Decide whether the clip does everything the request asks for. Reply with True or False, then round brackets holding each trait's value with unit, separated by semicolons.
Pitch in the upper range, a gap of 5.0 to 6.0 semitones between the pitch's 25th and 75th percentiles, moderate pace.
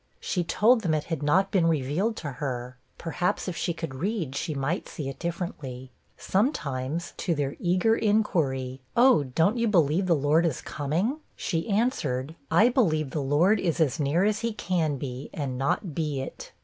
False (165 Hz; 5.5 semitones; 180 wpm)